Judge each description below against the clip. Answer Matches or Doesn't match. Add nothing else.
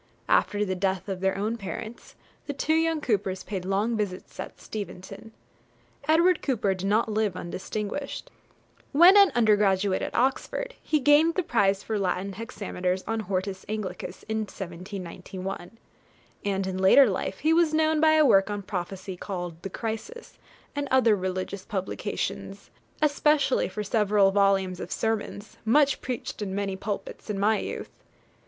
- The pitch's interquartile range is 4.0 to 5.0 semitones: Matches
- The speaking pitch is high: Matches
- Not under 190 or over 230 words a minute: Doesn't match